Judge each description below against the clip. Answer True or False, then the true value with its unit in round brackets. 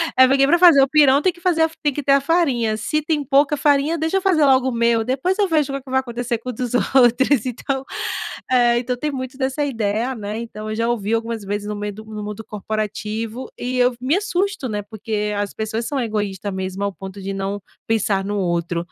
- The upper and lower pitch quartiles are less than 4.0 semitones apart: False (4.7 semitones)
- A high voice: True (240 Hz)